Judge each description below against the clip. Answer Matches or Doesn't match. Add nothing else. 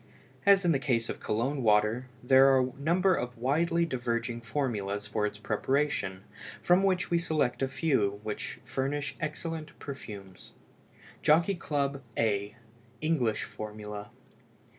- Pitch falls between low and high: Doesn't match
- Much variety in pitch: Matches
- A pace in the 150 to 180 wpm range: Doesn't match